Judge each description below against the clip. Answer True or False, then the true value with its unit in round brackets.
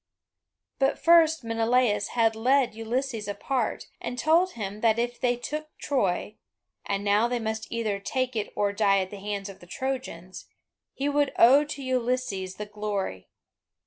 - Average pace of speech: True (160 wpm)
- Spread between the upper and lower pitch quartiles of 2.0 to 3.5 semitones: False (4.0 semitones)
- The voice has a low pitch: False (230 Hz)